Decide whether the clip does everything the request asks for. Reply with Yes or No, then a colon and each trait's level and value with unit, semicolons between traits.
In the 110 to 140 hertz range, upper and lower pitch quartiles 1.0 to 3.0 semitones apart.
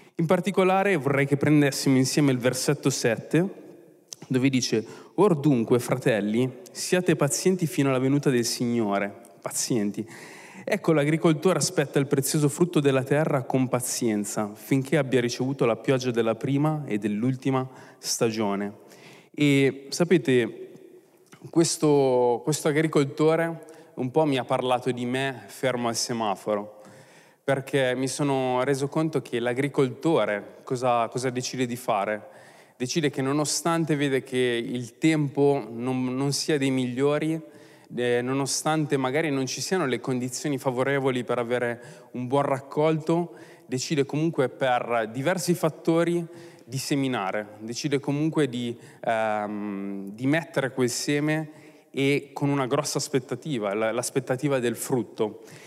No: low, 135 Hz; average, 3.7 semitones